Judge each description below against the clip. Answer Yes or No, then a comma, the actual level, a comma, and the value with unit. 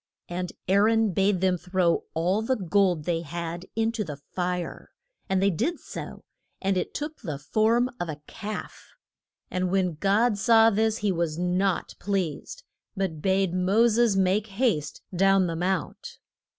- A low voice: No, high, 190 Hz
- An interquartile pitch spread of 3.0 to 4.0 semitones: Yes, average, 3.4 semitones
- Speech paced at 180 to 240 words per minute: No, average, 165 wpm